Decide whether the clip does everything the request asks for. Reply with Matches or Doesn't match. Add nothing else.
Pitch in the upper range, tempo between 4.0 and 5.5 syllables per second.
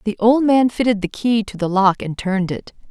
Matches